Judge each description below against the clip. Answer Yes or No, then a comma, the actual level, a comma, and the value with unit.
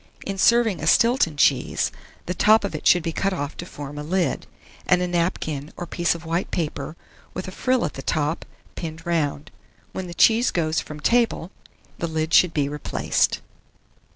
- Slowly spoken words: No, average, 185 wpm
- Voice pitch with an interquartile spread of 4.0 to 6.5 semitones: No, average, 3.5 semitones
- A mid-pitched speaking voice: Yes, medium, 170 Hz